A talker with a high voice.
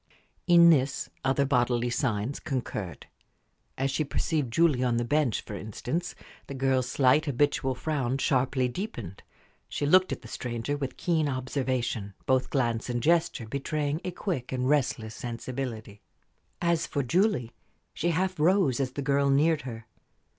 No: low, 135 Hz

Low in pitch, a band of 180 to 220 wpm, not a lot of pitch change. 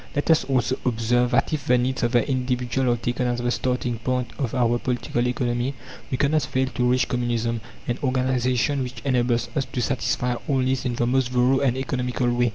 Yes: low, 125 Hz; fast, 205 wpm; narrow, 1.4 semitones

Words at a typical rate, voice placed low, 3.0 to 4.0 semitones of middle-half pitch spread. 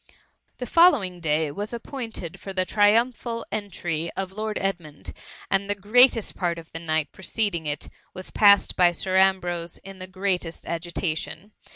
No: average, 165 wpm; high, 190 Hz; average, 3.6 semitones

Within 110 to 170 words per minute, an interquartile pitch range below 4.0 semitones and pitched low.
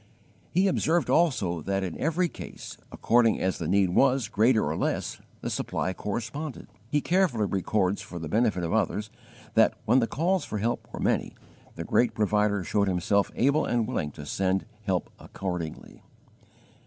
No: average, 165 wpm; wide, 5.6 semitones; low, 105 Hz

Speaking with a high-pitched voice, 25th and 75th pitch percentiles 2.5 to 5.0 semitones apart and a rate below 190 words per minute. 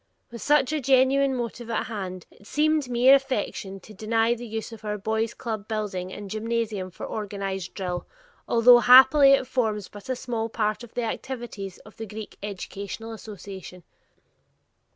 Yes: high, 225 Hz; average, 3.4 semitones; average, 165 wpm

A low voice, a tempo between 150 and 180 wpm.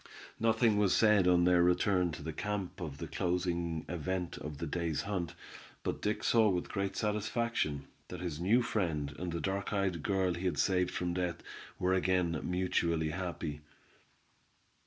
Yes: very low, 90 Hz; average, 165 wpm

